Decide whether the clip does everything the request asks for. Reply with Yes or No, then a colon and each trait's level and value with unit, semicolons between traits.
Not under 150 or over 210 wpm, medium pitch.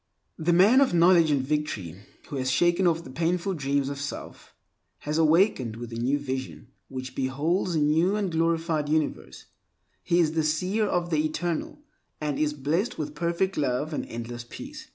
Yes: average, 175 wpm; medium, 155 Hz